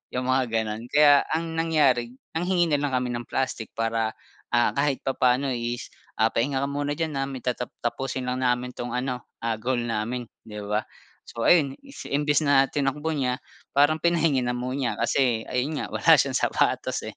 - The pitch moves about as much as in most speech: Yes, average, 3.1 semitones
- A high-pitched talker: No, low, 130 Hz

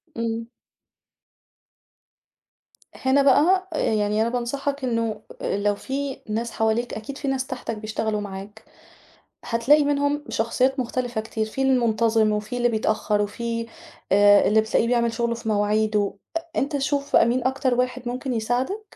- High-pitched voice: Yes, high, 235 Hz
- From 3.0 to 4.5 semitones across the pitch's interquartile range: Yes, average, 3.4 semitones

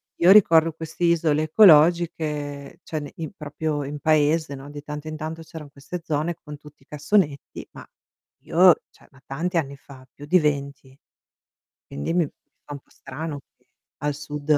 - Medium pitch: Yes, medium, 150 Hz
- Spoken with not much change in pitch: Yes, narrow, 2.1 semitones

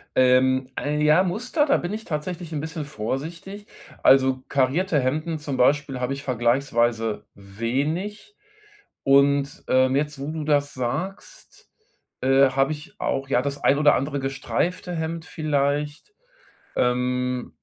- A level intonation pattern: No, average, 3.5 semitones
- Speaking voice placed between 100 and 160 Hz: Yes, medium, 140 Hz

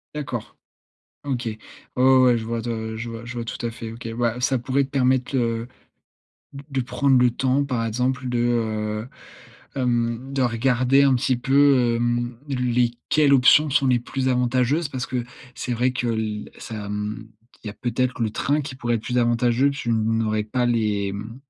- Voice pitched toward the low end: Yes, low, 120 Hz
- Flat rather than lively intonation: Yes, narrow, 2.2 semitones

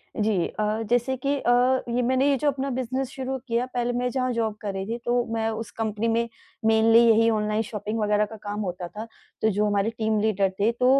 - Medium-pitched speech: No, high, 225 Hz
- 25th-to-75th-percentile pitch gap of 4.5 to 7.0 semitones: No, narrow, 2.5 semitones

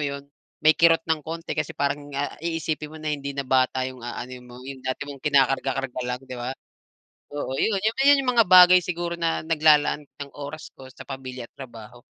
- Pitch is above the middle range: No, medium, 145 Hz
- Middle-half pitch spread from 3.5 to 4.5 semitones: Yes, average, 3.8 semitones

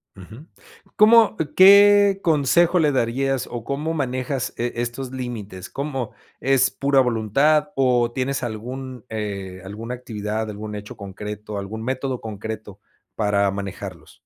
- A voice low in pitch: Yes, low, 120 Hz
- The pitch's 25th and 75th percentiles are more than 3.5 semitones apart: Yes, average, 4.5 semitones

